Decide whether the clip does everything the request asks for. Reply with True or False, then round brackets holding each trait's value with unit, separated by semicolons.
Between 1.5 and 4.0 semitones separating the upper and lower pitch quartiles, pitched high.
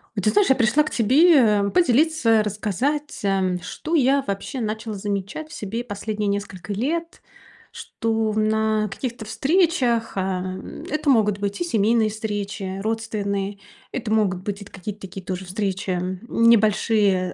True (3.1 semitones; 215 Hz)